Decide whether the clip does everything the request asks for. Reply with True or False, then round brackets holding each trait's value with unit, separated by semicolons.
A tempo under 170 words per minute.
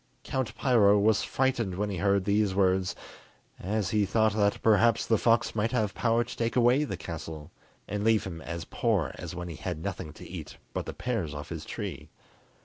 False (200 wpm)